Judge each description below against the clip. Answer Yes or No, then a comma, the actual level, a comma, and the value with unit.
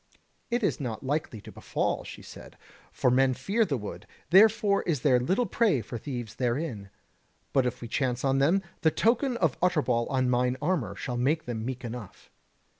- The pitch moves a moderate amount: No, wide, 6.2 semitones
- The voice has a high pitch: No, low, 135 Hz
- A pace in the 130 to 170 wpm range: No, average, 185 wpm